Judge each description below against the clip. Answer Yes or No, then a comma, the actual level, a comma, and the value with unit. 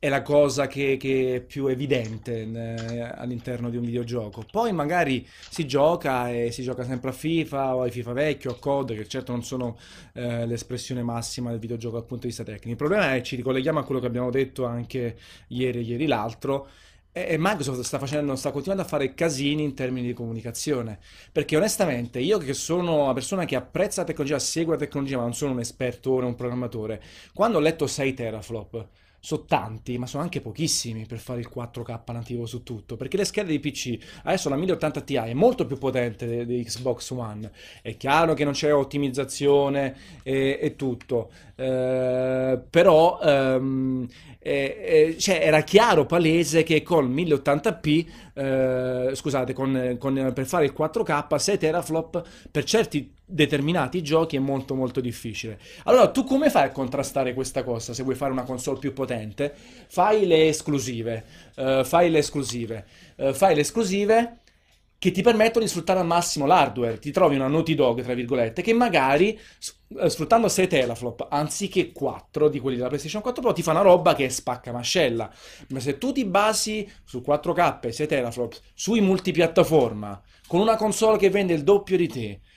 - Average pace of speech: No, fast, 180 wpm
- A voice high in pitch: No, low, 135 Hz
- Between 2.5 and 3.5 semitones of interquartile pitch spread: No, average, 4.7 semitones